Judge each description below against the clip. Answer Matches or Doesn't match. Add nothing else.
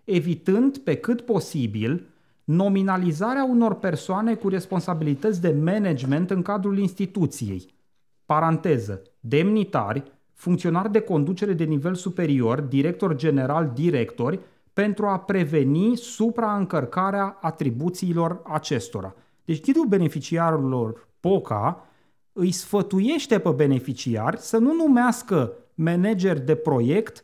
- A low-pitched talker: Doesn't match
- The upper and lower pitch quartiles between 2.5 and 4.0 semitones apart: Doesn't match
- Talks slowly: Matches